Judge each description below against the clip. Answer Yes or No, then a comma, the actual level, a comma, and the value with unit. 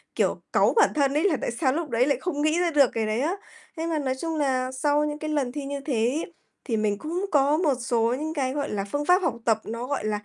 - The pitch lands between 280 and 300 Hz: Yes, very high, 285 Hz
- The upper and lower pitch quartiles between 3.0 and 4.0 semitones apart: Yes, average, 3.7 semitones